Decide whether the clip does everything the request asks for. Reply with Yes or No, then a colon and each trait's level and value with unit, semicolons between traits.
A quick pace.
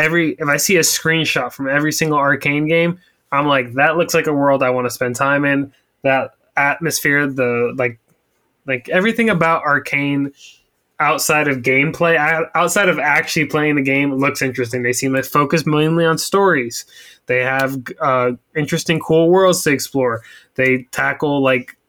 No: average, 170 wpm